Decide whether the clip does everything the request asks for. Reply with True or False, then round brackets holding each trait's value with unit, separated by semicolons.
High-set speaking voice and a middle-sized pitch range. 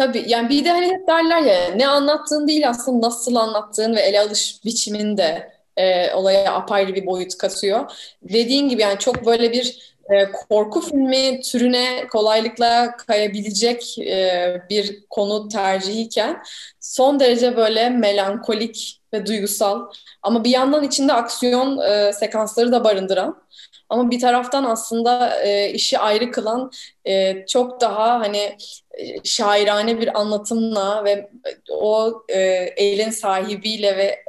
True (225 Hz; 3.3 semitones)